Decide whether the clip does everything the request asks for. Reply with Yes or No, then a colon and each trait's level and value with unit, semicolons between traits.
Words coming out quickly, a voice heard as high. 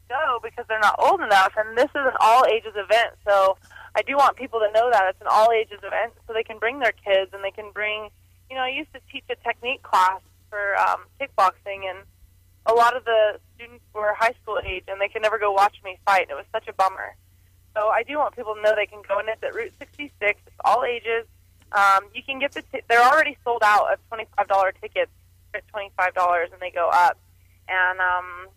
Yes: fast, 240 wpm; high, 210 Hz